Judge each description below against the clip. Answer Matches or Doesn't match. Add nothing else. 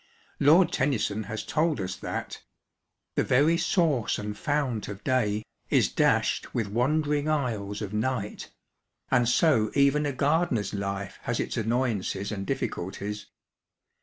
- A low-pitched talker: Matches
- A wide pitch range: Matches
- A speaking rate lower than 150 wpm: Matches